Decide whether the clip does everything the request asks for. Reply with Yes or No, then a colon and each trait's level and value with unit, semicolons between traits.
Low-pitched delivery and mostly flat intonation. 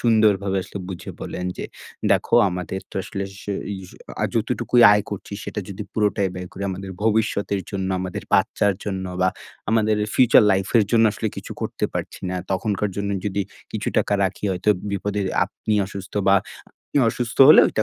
Yes: low, 100 Hz; narrow, 2.0 semitones